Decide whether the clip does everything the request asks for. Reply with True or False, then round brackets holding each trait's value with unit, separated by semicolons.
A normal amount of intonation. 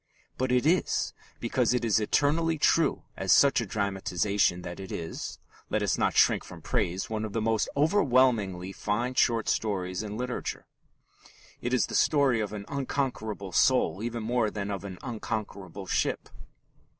True (4.1 semitones)